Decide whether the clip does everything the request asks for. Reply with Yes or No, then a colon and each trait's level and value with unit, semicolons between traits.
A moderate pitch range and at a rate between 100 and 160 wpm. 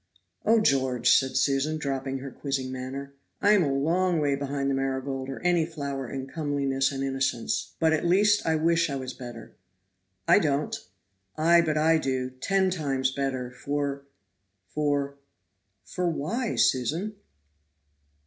Yes: average, 3.2 semitones; average, 150 wpm